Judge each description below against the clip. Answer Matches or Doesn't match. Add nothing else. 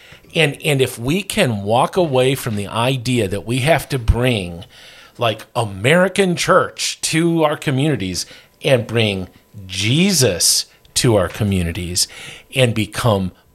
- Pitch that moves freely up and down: Matches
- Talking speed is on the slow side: Matches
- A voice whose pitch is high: Doesn't match